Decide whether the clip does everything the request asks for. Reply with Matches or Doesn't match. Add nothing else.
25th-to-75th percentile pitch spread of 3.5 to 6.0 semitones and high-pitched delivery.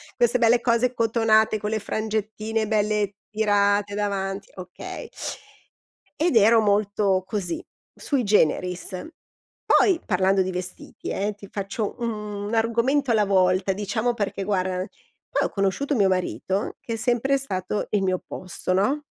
Doesn't match